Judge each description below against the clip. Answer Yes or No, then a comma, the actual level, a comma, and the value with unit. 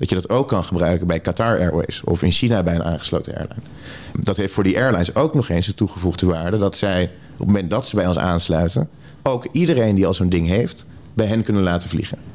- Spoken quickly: Yes, fast, 245 wpm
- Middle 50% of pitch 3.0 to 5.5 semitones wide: Yes, average, 3.8 semitones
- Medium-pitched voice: No, very low, 95 Hz